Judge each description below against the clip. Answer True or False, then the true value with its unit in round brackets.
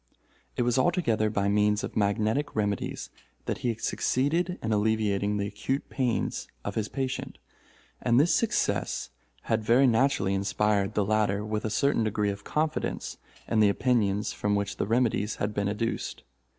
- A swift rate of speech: False (165 wpm)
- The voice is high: False (110 Hz)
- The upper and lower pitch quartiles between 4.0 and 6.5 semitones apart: False (3.3 semitones)